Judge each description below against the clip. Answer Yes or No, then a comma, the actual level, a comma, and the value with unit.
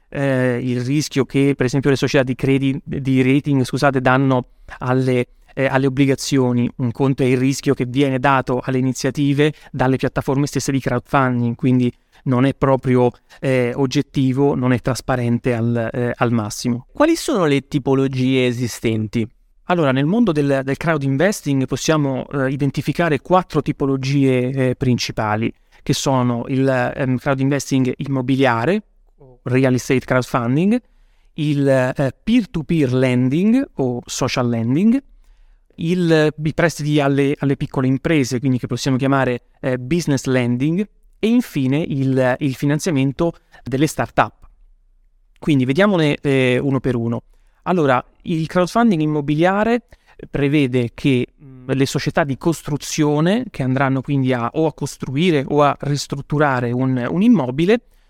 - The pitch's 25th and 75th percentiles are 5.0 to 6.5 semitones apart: No, narrow, 2.6 semitones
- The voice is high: No, low, 135 Hz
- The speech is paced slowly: No, average, 135 wpm